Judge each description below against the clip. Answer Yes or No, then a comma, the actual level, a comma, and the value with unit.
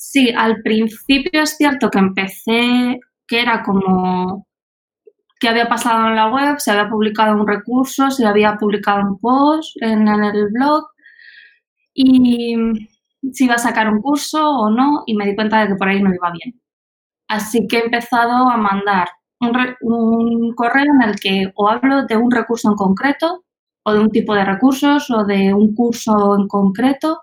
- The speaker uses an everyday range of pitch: Yes, average, 3.8 semitones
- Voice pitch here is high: Yes, high, 230 Hz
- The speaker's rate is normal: Yes, average, 180 wpm